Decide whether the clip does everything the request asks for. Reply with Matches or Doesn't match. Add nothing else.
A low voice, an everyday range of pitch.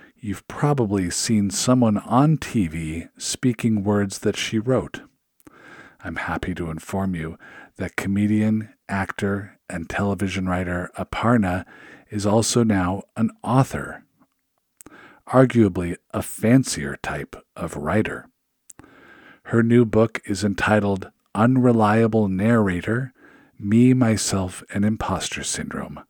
Matches